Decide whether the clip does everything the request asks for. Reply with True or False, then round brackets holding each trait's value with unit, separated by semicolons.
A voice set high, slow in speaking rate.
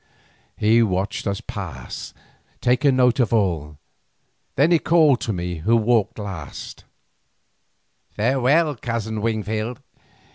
False (110 Hz; 110 wpm)